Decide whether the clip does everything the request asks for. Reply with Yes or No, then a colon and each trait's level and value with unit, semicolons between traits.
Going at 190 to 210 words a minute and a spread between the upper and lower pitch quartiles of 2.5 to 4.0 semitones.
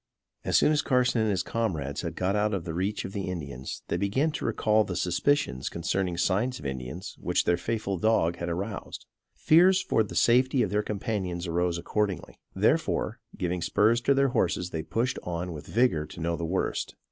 No: average, 195 wpm; average, 4.8 semitones